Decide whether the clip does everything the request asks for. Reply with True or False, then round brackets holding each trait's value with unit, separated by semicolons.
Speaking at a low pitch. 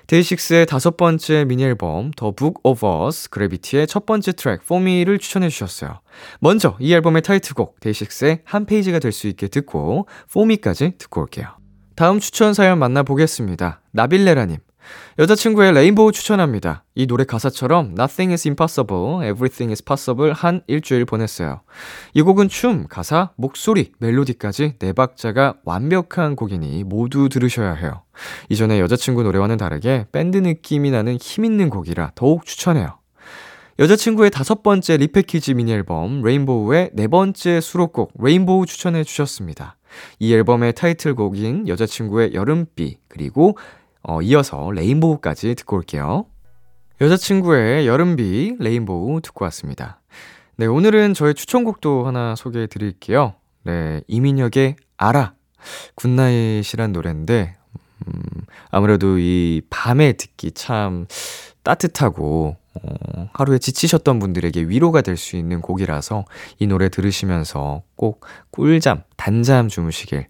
True (130 Hz)